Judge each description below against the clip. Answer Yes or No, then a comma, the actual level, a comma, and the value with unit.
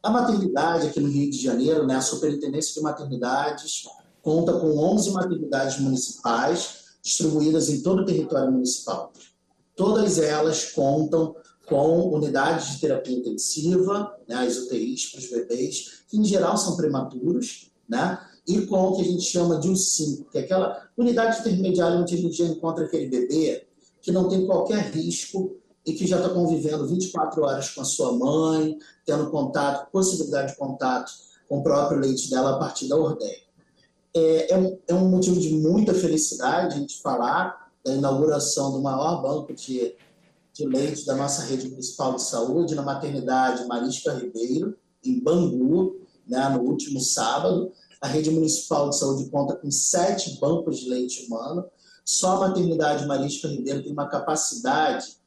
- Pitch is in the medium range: Yes, medium, 155 Hz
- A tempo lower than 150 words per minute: No, average, 165 wpm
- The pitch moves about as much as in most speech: Yes, average, 4.9 semitones